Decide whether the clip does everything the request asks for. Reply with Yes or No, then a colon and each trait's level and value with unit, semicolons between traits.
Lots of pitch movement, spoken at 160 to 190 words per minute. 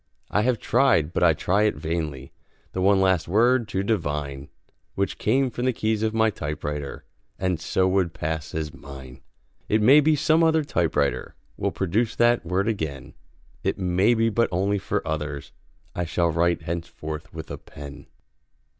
Yes: wide, 6.0 semitones; average, 170 wpm